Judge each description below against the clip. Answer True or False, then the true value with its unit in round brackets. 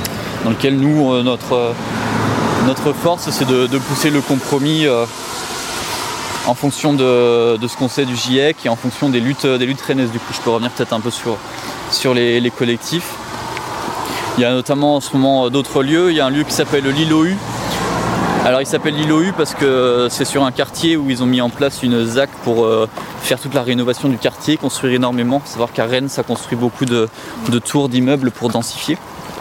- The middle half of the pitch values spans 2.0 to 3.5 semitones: True (2.8 semitones)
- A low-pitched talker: True (130 Hz)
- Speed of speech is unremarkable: True (200 wpm)